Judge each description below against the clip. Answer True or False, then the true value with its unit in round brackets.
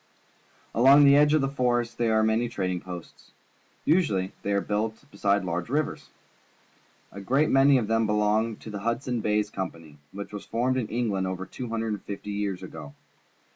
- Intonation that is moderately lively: True (3.5 semitones)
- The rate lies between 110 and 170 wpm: False (180 wpm)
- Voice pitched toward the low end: True (110 Hz)